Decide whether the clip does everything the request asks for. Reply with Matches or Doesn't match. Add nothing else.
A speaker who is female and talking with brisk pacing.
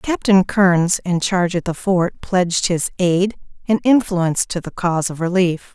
Doesn't match